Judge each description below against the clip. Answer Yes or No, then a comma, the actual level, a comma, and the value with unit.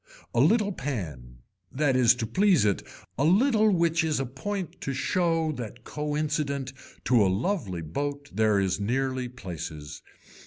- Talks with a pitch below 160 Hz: Yes, low, 135 Hz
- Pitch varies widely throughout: Yes, wide, 7.1 semitones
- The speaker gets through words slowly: No, average, 155 wpm